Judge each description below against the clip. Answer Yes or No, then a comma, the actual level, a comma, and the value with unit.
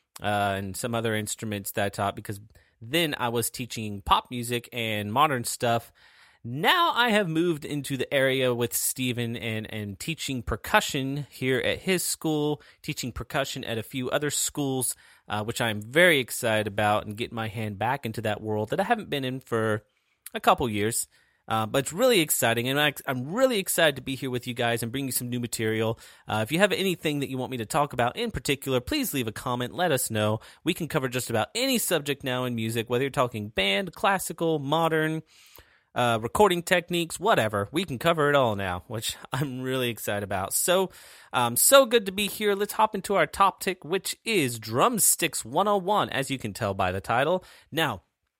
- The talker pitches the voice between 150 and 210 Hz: No, low, 130 Hz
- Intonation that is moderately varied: No, wide, 6.6 semitones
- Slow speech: No, average, 200 wpm